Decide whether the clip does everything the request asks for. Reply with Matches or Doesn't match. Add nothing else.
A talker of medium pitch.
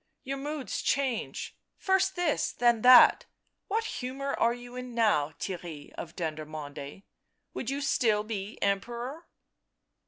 Doesn't match